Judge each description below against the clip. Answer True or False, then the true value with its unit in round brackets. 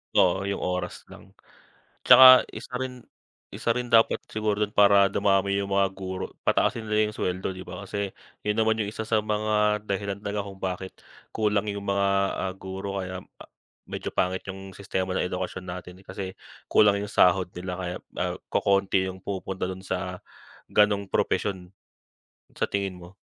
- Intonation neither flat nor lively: False (1.8 semitones)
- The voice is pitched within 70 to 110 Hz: True (100 Hz)